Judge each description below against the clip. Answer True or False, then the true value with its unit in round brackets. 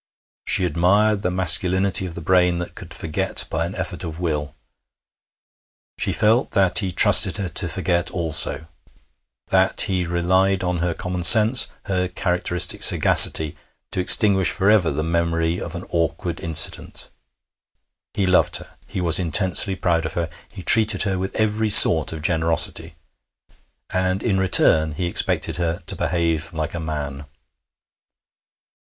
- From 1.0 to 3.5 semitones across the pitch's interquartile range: True (2.4 semitones)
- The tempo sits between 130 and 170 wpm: True (150 wpm)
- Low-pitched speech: True (90 Hz)